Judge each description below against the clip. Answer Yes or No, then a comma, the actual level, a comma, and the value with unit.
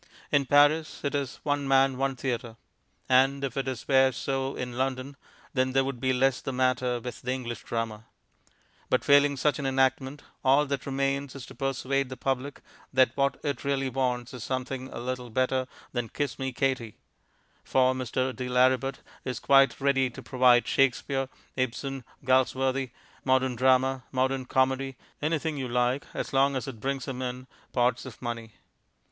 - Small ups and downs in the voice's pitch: Yes, narrow, 1.3 semitones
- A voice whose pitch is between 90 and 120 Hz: No, low, 130 Hz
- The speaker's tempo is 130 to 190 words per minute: Yes, average, 170 wpm